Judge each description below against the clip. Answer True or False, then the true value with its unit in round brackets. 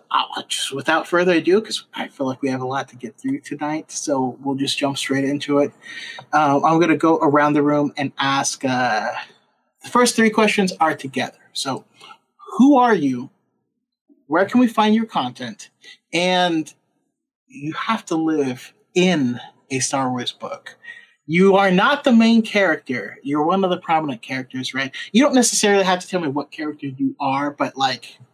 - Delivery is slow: False (185 wpm)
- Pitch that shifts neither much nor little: False (7.8 semitones)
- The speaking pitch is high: False (155 Hz)